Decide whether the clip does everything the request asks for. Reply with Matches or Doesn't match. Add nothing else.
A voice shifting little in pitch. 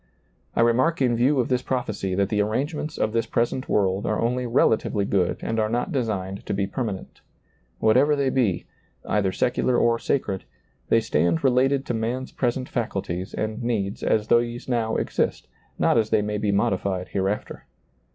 Doesn't match